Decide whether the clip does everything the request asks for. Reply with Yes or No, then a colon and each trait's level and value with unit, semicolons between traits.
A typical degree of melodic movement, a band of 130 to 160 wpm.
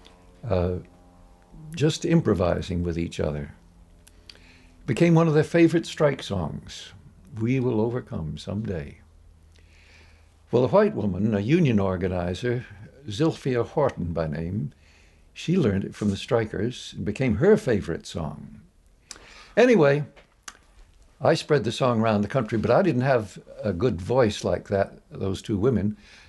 No: wide, 6.8 semitones; slow, 135 wpm